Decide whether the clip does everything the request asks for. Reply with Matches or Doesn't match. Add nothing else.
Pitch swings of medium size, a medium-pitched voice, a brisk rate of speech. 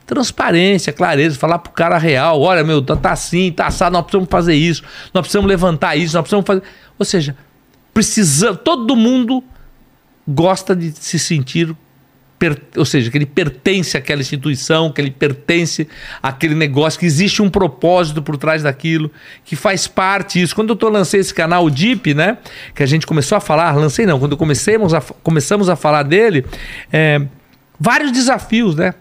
Doesn't match